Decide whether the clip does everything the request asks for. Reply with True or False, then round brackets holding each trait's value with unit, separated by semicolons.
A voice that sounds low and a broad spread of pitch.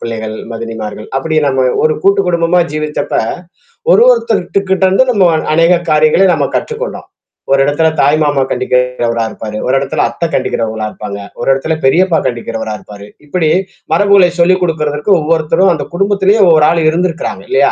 False (155 Hz; 6.1 semitones)